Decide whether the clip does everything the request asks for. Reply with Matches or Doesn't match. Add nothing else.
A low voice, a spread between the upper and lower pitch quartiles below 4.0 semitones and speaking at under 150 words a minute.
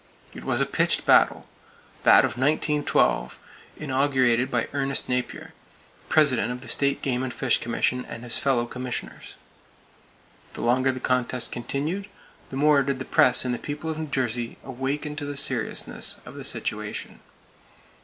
Doesn't match